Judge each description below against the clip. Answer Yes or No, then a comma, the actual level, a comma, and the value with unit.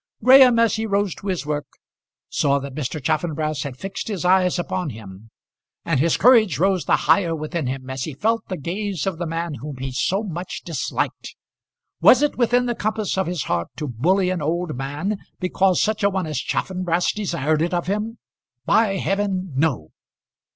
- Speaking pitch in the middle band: Yes, medium, 175 Hz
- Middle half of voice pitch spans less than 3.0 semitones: No, average, 4.9 semitones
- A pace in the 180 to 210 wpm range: Yes, average, 185 wpm